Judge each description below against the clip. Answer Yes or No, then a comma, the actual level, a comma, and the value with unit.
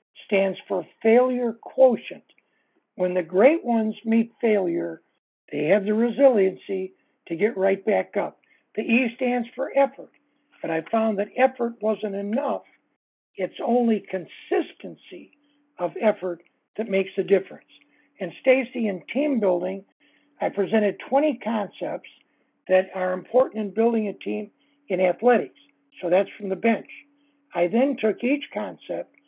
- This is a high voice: Yes, high, 220 Hz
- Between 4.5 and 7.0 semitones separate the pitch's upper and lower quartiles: Yes, wide, 5.4 semitones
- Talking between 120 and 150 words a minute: Yes, average, 140 wpm